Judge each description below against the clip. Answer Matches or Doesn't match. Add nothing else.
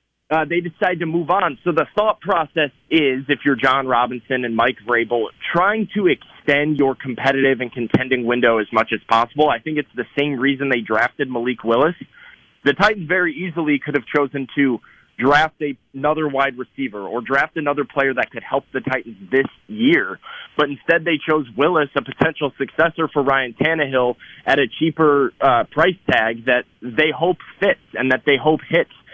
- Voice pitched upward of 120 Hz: Matches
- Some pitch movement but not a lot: Matches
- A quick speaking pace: Doesn't match